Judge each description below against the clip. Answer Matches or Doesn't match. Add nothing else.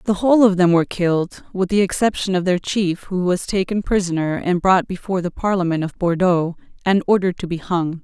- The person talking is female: Matches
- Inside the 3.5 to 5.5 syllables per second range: Doesn't match